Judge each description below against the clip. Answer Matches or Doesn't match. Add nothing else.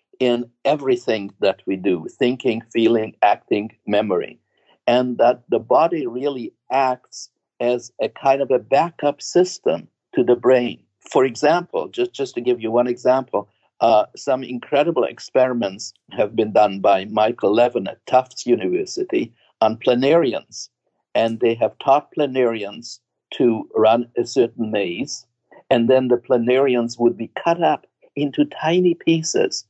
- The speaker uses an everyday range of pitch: Matches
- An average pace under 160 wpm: Matches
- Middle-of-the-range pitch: Doesn't match